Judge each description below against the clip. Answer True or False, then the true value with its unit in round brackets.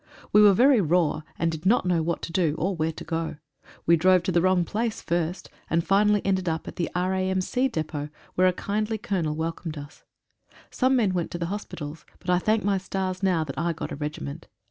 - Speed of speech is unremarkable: False (210 wpm)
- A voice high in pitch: False (180 Hz)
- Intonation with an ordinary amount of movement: True (3.2 semitones)